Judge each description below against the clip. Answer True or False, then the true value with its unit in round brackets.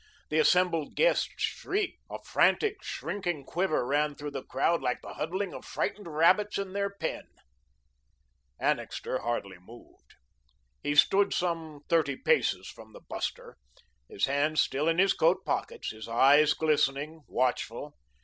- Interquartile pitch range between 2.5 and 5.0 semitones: True (4.7 semitones)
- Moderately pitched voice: True (155 Hz)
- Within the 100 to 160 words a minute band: True (140 wpm)